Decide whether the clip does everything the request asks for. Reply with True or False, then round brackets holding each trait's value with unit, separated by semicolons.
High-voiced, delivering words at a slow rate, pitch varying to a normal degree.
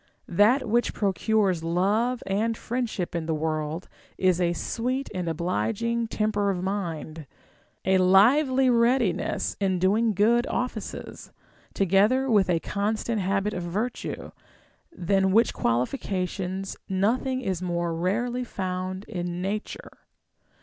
True (195 Hz; 120 wpm; 4.2 semitones)